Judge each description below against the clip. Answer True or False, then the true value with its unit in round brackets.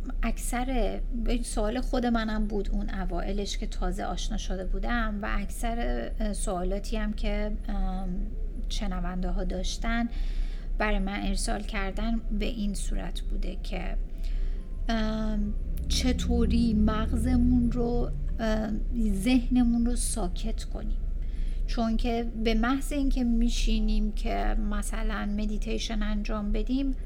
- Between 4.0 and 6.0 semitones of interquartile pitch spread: False (3.4 semitones)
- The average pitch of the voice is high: True (210 Hz)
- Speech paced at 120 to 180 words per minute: False (105 wpm)